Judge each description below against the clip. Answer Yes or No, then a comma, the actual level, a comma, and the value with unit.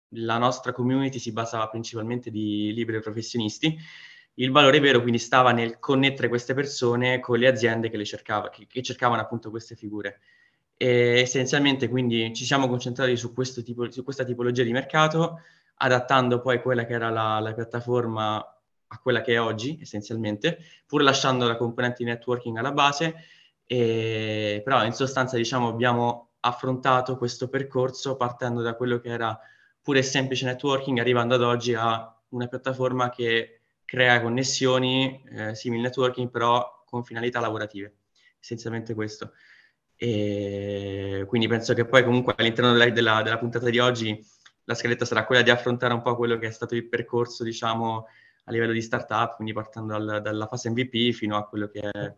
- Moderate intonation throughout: No, narrow, 1.9 semitones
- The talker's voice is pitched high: No, low, 120 Hz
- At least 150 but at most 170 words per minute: Yes, average, 165 wpm